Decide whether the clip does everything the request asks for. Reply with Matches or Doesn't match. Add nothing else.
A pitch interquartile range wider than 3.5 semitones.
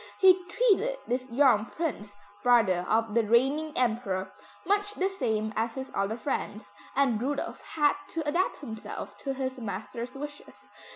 Matches